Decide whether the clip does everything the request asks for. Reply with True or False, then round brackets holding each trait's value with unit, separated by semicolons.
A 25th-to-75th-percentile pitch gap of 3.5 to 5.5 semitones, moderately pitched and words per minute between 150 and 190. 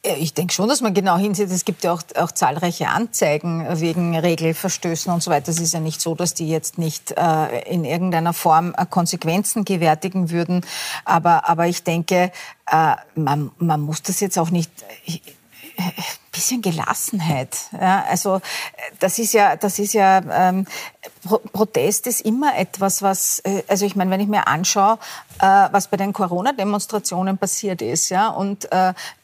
False (2.9 semitones; 180 Hz; 170 wpm)